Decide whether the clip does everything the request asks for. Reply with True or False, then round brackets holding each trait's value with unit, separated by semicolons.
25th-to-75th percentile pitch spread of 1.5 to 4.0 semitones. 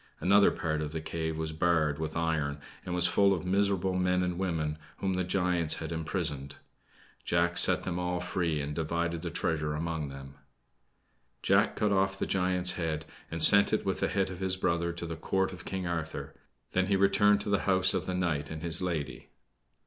True (2.8 semitones)